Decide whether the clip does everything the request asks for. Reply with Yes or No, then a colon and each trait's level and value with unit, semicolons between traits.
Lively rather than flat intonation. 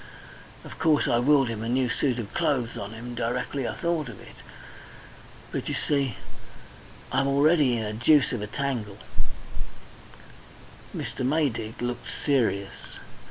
No: average, 3.6 semitones